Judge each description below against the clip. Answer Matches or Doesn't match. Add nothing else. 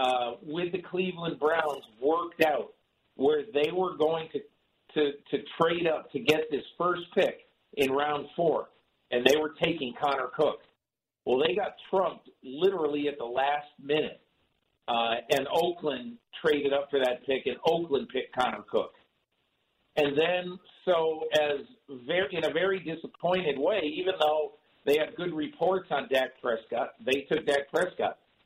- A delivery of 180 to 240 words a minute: Doesn't match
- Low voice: Doesn't match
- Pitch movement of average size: Matches